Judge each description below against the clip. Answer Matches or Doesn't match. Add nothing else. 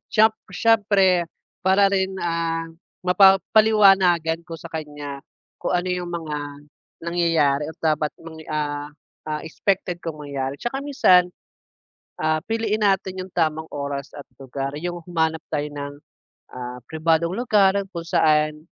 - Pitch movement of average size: Matches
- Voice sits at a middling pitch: Matches